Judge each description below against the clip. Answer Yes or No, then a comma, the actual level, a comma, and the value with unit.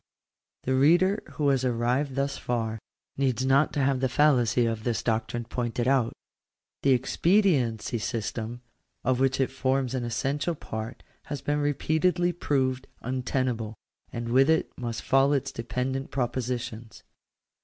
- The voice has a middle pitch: No, low, 130 Hz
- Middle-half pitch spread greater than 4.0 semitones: No, average, 2.7 semitones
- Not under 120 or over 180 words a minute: Yes, average, 140 wpm